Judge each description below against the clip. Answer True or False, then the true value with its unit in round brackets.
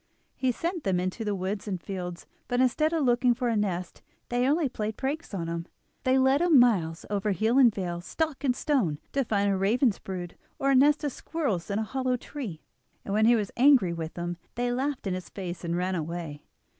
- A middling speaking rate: False (220 wpm)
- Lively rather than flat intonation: True (6.4 semitones)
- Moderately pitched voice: False (220 Hz)